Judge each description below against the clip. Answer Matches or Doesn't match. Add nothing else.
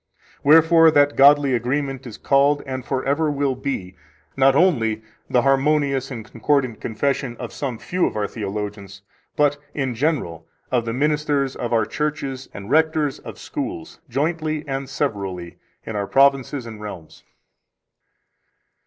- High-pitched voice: Doesn't match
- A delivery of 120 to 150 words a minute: Matches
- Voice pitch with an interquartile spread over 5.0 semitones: Doesn't match